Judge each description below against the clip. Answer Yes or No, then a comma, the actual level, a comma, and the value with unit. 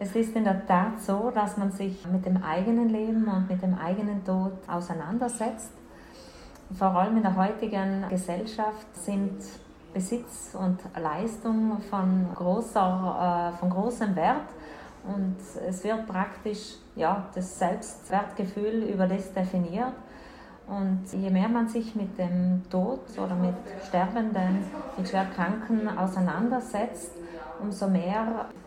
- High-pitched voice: Yes, high, 195 Hz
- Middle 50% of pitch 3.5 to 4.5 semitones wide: No, average, 2.9 semitones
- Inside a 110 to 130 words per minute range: Yes, slow, 125 wpm